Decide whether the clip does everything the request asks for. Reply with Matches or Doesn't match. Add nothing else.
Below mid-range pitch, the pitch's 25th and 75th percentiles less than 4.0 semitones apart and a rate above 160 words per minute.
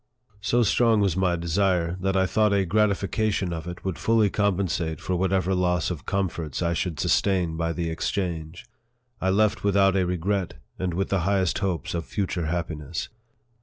Matches